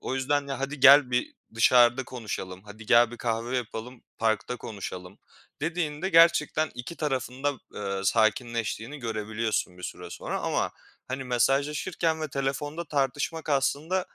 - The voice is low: Yes, low, 130 Hz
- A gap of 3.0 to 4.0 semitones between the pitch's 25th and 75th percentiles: No, average, 4.5 semitones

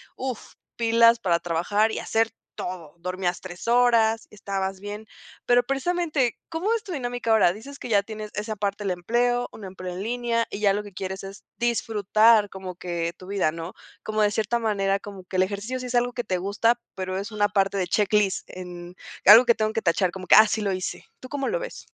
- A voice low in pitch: No, high, 210 Hz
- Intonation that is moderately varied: Yes, average, 3.7 semitones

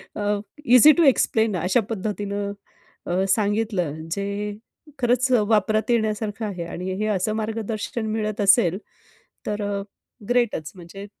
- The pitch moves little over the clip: Yes, narrow, 2.2 semitones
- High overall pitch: Yes, high, 210 Hz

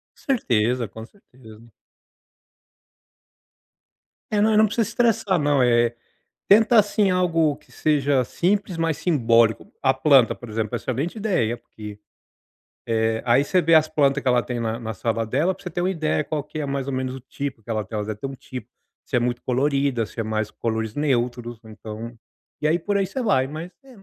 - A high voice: No, low, 135 Hz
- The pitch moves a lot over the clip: Yes, wide, 6.3 semitones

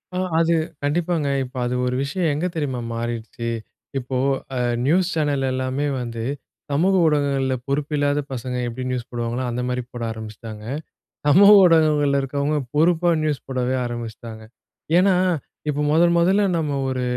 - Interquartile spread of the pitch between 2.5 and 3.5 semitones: No, average, 4.0 semitones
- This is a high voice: No, medium, 140 Hz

